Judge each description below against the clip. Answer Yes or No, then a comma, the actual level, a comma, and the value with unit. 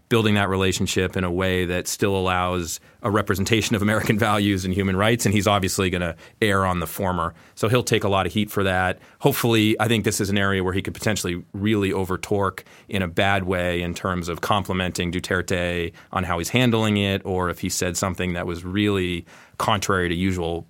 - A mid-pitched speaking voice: No, very low, 95 Hz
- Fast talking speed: Yes, fast, 210 wpm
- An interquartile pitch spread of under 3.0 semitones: Yes, narrow, 2.5 semitones